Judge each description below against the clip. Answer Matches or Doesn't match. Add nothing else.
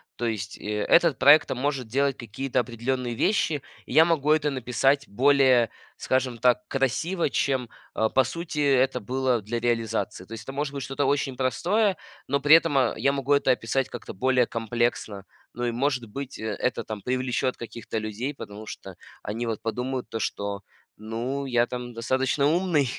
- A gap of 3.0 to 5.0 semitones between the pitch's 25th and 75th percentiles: Matches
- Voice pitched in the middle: Doesn't match